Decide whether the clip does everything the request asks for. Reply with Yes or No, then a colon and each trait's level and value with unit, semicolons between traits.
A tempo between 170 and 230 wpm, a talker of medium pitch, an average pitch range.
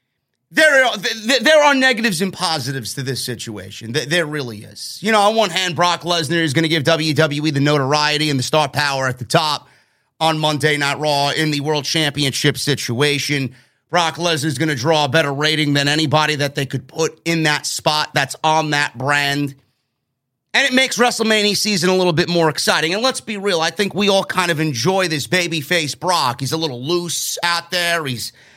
Yes: average, 200 wpm; medium, 155 Hz; average, 3.7 semitones